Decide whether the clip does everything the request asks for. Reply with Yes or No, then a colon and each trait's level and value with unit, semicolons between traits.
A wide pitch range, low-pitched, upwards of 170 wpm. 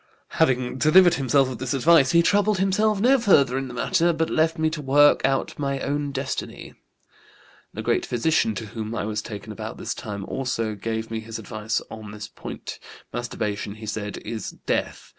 Yes: wide, 6.2 semitones; low, 130 Hz; average, 185 wpm